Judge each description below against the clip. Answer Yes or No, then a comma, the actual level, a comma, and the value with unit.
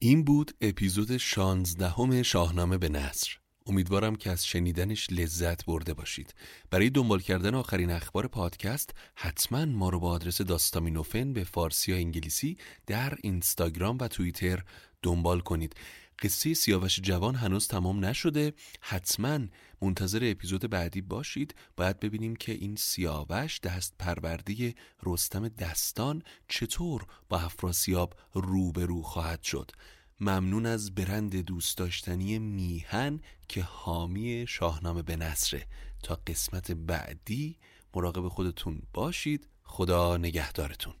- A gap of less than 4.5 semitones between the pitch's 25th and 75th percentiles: Yes, average, 4.1 semitones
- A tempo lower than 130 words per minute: Yes, average, 120 wpm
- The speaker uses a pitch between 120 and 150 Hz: No, very low, 95 Hz